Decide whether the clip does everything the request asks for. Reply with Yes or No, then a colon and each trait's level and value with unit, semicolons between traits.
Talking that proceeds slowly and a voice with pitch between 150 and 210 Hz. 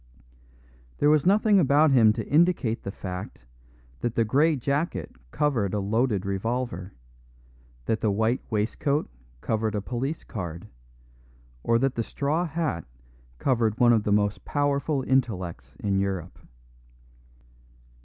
No: slow, 130 wpm; low, 115 Hz